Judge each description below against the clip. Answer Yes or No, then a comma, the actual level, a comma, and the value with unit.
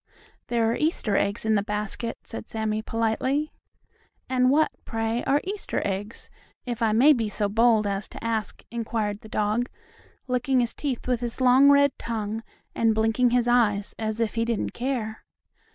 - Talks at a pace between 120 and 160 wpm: No, average, 170 wpm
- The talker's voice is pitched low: No, high, 230 Hz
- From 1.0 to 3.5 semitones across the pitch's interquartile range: Yes, narrow, 2.5 semitones